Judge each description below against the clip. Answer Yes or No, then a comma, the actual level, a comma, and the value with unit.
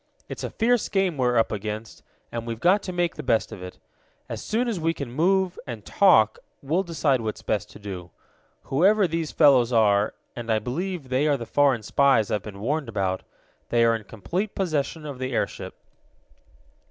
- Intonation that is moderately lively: No, wide, 7.5 semitones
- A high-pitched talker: No, low, 130 Hz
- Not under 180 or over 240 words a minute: Yes, average, 190 wpm